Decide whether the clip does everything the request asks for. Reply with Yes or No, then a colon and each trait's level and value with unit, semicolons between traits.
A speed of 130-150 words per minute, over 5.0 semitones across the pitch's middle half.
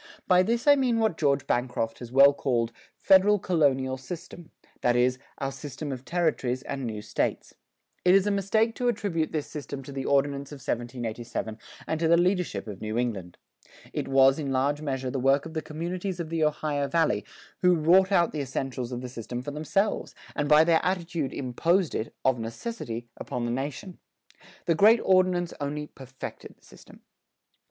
No: average, 180 wpm; wide, 5.4 semitones